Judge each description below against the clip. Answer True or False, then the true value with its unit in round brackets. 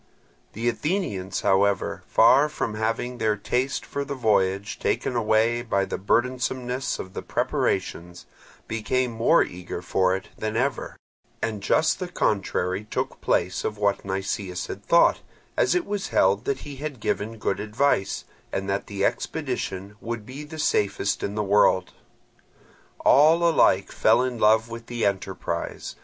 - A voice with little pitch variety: False (4.5 semitones)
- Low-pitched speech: True (110 Hz)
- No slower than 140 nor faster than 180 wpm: True (150 wpm)